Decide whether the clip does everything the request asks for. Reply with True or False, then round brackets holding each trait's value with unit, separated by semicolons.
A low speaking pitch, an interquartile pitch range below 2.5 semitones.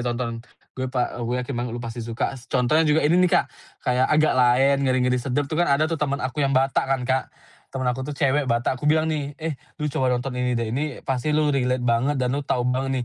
False (130 Hz; 2.8 semitones)